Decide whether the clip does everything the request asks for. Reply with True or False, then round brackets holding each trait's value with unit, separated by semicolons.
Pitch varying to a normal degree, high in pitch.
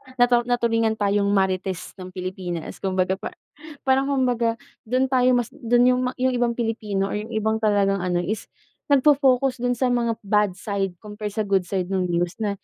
True (4.1 semitones; 215 Hz)